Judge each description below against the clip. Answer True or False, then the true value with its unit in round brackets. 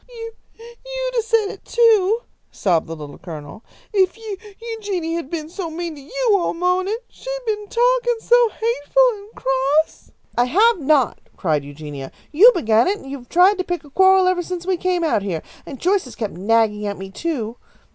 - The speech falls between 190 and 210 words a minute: True (200 wpm)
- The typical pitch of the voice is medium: False (355 Hz)